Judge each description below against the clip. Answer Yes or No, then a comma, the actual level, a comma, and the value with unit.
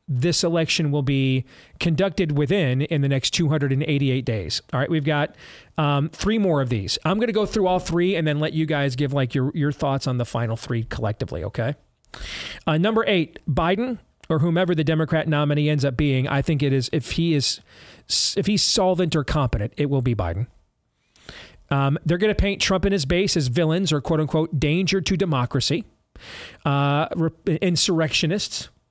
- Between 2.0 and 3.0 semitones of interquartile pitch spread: No, average, 4.0 semitones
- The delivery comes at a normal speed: Yes, average, 185 wpm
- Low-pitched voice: No, medium, 155 Hz